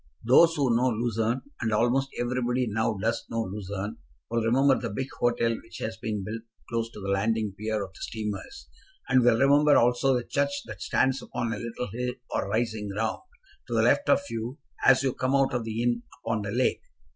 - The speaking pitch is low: Yes, low, 115 Hz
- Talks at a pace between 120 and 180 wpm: No, fast, 205 wpm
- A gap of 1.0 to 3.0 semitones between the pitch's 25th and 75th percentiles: Yes, narrow, 2.6 semitones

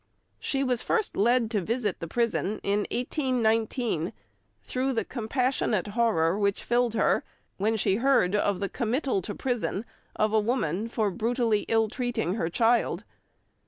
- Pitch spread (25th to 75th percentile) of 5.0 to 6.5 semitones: No, average, 3.2 semitones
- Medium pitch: No, high, 225 Hz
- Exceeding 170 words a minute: No, average, 150 wpm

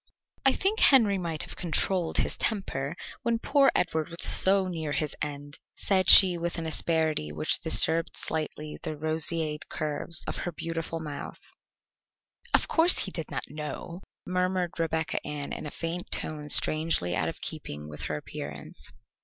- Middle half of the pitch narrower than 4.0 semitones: Yes, average, 3.3 semitones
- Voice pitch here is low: No, medium, 160 Hz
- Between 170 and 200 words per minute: No, average, 160 wpm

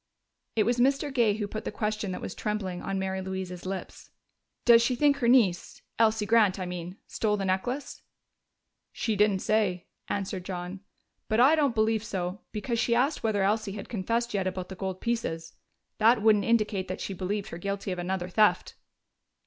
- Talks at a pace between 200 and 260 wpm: No, average, 185 wpm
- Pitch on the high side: Yes, high, 205 Hz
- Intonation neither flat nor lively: Yes, average, 3.4 semitones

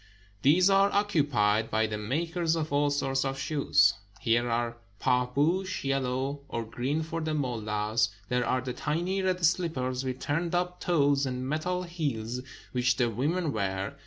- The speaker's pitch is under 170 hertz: Yes, low, 135 Hz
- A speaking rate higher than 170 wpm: No, average, 160 wpm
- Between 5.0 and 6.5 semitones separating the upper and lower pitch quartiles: Yes, wide, 5.4 semitones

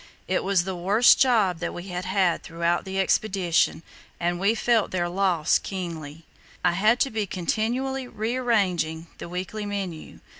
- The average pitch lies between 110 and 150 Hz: No, high, 190 Hz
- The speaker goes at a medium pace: Yes, average, 155 wpm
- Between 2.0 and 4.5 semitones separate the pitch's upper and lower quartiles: Yes, average, 3.8 semitones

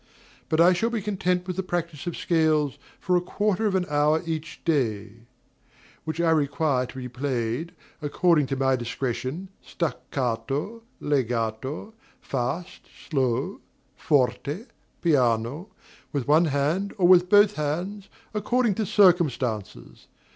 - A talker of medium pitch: Yes, medium, 155 Hz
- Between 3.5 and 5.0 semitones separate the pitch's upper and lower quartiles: No, wide, 5.5 semitones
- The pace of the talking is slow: Yes, slow, 130 wpm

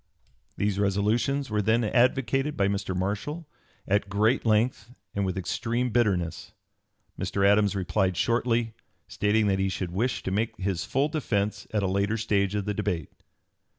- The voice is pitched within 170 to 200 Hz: No, low, 105 Hz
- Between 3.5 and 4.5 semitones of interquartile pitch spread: No, average, 3.0 semitones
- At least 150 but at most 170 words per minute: Yes, average, 160 wpm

